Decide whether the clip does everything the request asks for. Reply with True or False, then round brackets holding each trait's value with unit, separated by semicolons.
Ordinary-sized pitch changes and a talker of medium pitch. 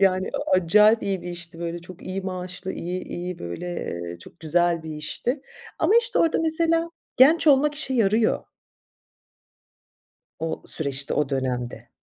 False (6.1 semitones; 180 Hz)